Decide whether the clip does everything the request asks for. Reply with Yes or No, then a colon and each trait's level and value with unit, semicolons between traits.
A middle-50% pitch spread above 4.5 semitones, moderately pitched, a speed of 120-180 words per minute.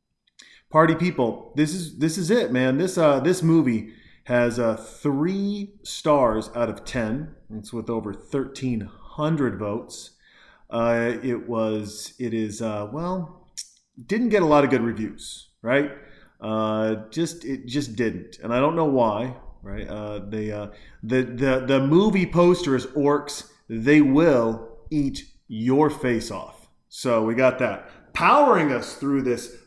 No: wide, 5.4 semitones; low, 125 Hz; average, 150 wpm